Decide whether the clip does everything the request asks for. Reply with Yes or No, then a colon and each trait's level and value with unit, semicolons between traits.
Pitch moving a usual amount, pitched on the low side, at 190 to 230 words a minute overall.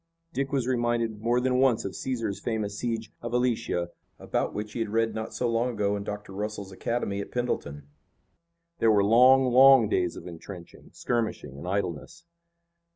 No: average, 3.3 semitones; low, 115 Hz; average, 170 wpm